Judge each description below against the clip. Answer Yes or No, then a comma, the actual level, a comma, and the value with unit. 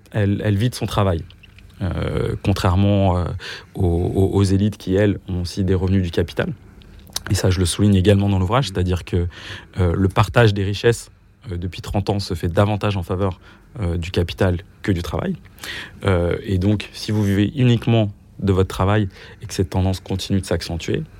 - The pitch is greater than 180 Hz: No, low, 100 Hz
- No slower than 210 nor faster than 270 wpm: No, average, 190 wpm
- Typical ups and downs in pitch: No, narrow, 1.8 semitones